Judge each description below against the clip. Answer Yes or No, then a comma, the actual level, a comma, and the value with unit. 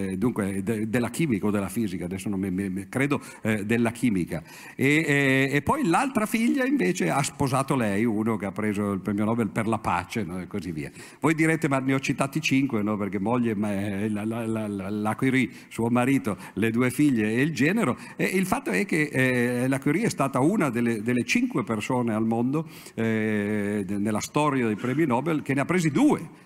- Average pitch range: Yes, average, 5.0 semitones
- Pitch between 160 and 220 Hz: No, low, 120 Hz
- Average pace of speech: No, fast, 200 wpm